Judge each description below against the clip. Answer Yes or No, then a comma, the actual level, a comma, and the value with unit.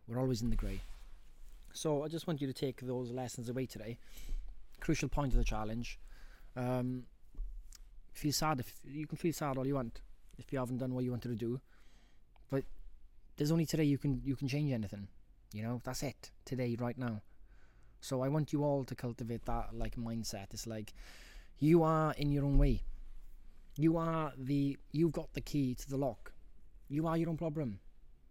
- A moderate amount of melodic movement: Yes, average, 4.0 semitones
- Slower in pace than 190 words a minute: No, average, 195 wpm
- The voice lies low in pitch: Yes, low, 125 Hz